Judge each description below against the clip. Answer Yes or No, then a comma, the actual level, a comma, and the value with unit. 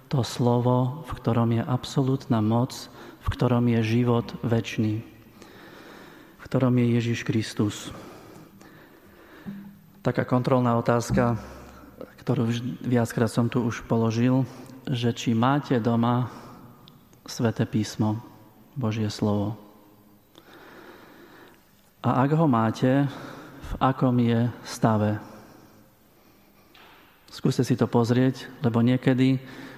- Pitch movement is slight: Yes, narrow, 2.2 semitones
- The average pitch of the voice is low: Yes, low, 120 Hz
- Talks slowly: Yes, slow, 95 wpm